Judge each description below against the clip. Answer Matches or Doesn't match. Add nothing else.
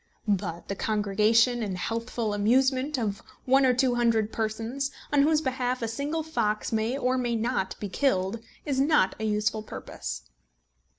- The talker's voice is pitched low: Doesn't match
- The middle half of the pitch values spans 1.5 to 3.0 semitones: Doesn't match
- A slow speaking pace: Doesn't match